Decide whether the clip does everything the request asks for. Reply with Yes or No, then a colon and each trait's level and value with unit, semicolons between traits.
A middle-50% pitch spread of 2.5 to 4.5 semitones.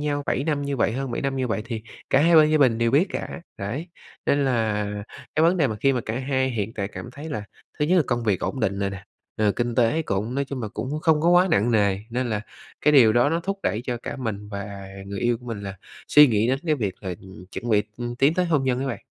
No: average, 5.1 semitones